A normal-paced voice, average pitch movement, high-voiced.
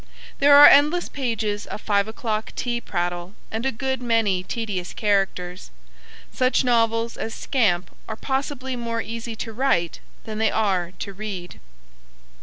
Yes: average, 145 wpm; average, 3.7 semitones; high, 225 Hz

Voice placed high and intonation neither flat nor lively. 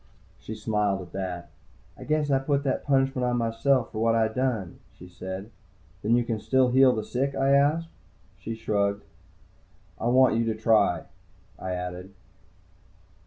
No: low, 115 Hz; average, 4.7 semitones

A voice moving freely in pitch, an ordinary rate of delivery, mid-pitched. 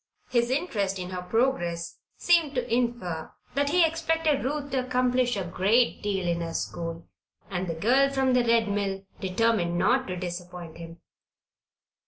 No: wide, 6.4 semitones; average, 160 wpm; high, 225 Hz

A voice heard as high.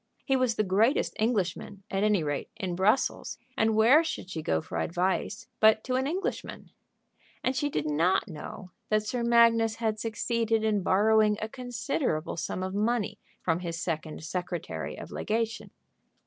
Yes: high, 215 Hz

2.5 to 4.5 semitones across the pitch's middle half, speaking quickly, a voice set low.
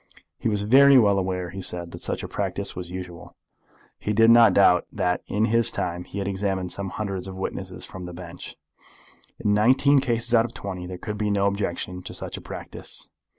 Yes: average, 3.1 semitones; fast, 210 wpm; low, 100 Hz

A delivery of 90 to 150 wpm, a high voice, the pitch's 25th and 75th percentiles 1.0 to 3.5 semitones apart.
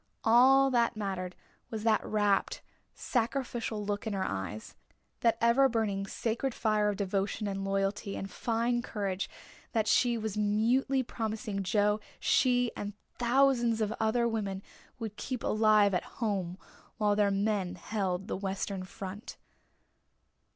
Yes: slow, 135 wpm; high, 215 Hz; average, 2.9 semitones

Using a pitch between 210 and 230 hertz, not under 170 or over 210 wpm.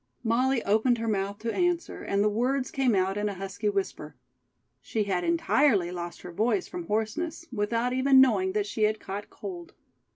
Yes: high, 215 Hz; average, 185 wpm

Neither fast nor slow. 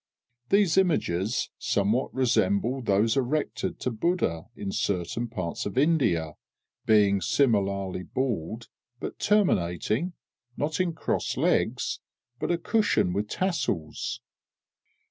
No: slow, 105 wpm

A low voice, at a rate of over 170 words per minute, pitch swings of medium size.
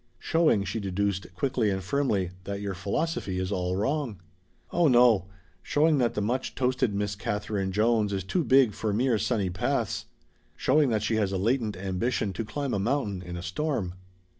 Yes: low, 105 Hz; average, 180 wpm; average, 4.9 semitones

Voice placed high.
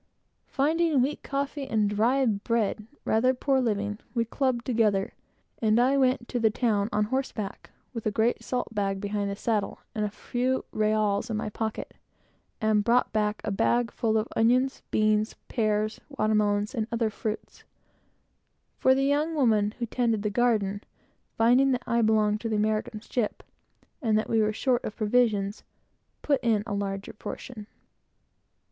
Yes: high, 220 Hz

